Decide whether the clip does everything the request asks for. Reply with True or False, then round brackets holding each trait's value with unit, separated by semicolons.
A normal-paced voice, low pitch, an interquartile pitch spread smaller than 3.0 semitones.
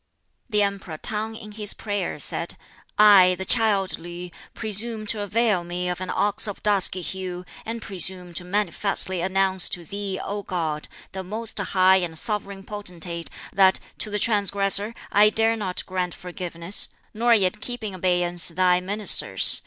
False (160 wpm; 195 Hz; 2.6 semitones)